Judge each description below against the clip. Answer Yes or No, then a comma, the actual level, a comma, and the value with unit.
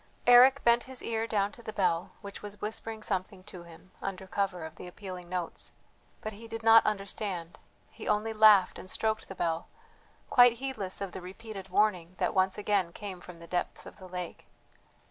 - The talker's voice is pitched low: No, high, 200 Hz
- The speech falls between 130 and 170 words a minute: No, average, 190 wpm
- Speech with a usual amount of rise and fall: Yes, average, 3.2 semitones